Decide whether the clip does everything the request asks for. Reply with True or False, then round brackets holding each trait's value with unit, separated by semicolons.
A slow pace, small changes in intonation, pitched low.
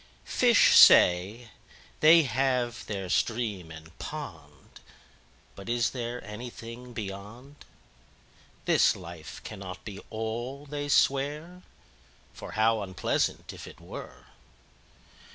False (90 wpm; 4.6 semitones; 115 Hz)